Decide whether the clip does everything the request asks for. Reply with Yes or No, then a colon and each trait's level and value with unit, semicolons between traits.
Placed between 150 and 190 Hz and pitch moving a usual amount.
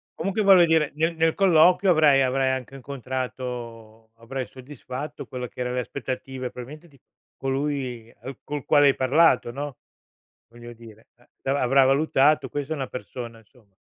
No: low, 135 Hz; average, 3.1 semitones